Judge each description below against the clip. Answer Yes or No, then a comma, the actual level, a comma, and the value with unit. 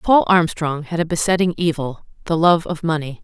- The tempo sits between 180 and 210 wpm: No, average, 165 wpm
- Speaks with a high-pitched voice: No, medium, 165 Hz